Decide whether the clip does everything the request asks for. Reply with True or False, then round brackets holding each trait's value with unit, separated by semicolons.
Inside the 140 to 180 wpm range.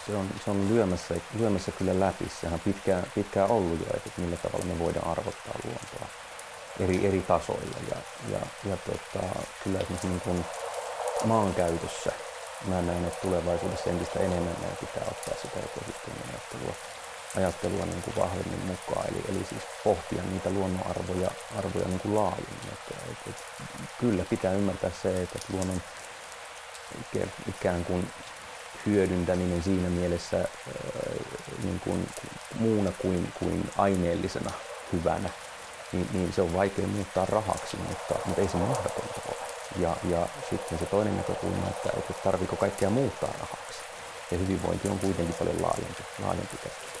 True (145 wpm)